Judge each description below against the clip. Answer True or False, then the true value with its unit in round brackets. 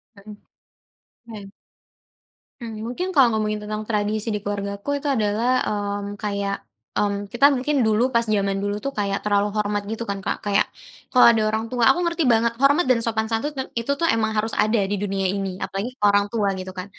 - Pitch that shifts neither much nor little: False (2.3 semitones)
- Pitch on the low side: False (215 Hz)